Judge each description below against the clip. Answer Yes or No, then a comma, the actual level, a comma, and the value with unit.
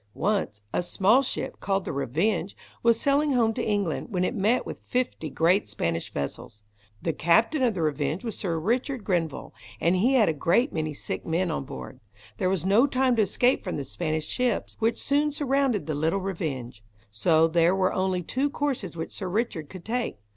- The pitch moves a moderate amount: No, wide, 6.8 semitones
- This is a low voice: No, high, 190 Hz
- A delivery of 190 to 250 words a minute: Yes, average, 195 wpm